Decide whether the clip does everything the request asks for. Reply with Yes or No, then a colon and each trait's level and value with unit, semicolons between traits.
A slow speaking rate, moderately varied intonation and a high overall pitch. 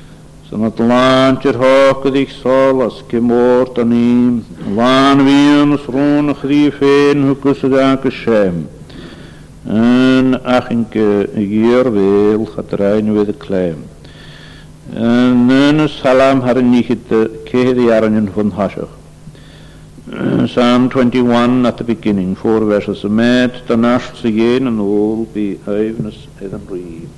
No: slow, 130 wpm; average, 3.3 semitones; low, 120 Hz